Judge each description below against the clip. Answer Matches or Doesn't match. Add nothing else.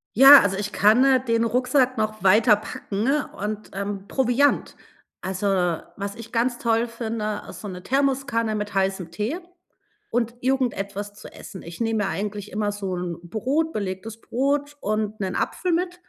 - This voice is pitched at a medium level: Doesn't match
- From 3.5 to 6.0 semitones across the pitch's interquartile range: Matches